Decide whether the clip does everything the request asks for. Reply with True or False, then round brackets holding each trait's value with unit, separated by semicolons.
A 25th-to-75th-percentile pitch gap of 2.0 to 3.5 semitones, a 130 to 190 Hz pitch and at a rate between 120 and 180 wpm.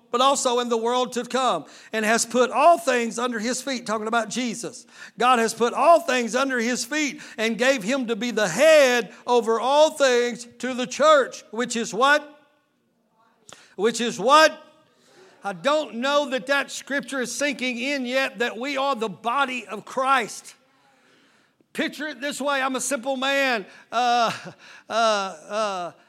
False (3.2 semitones; 250 Hz; 170 wpm)